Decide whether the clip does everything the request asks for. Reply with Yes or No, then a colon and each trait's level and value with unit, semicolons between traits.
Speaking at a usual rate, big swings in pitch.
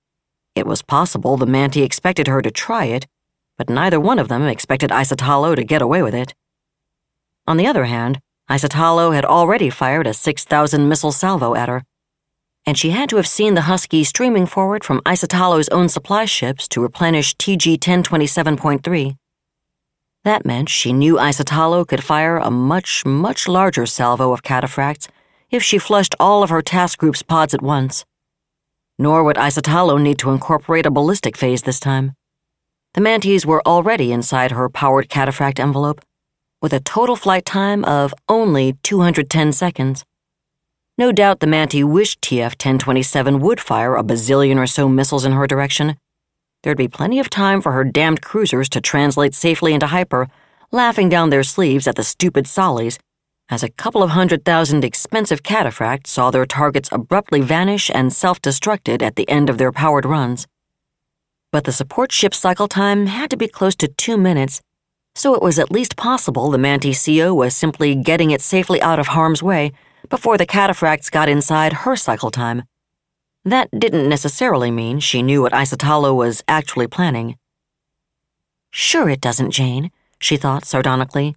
No: average, 170 wpm; average, 4.4 semitones